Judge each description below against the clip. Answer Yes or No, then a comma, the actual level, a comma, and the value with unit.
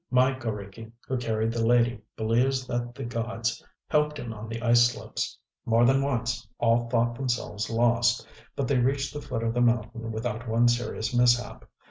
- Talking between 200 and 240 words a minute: No, average, 175 wpm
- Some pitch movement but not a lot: No, narrow, 1.3 semitones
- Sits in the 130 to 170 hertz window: No, low, 120 Hz